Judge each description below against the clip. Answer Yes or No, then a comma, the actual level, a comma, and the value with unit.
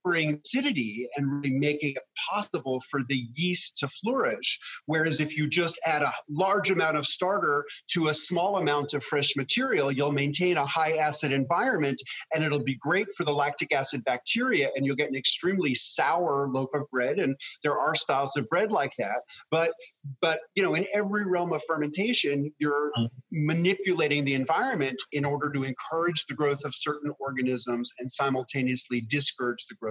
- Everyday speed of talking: Yes, average, 175 wpm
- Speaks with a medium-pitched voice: Yes, medium, 145 Hz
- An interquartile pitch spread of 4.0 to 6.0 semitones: No, average, 3.4 semitones